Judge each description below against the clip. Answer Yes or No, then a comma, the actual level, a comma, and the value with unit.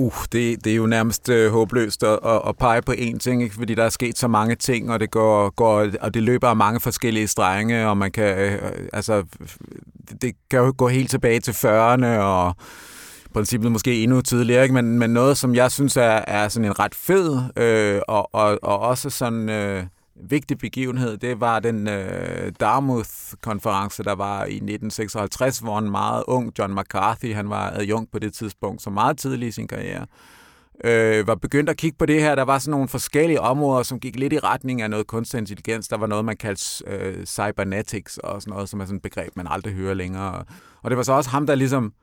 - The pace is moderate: Yes, average, 215 wpm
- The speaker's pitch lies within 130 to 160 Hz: No, low, 115 Hz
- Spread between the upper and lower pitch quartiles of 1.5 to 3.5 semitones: Yes, average, 3.2 semitones